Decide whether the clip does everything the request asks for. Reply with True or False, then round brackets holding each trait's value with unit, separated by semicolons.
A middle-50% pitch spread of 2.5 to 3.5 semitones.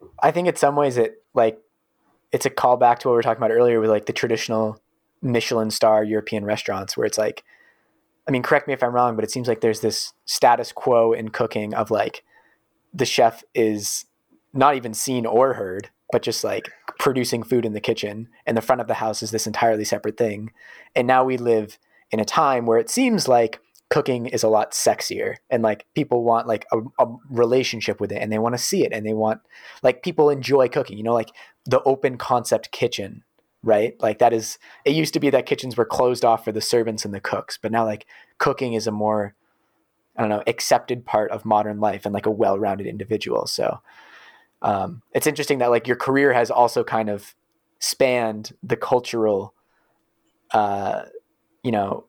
True (3.0 semitones)